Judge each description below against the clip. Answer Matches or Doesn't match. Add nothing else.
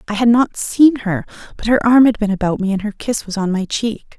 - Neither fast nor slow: Doesn't match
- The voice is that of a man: Doesn't match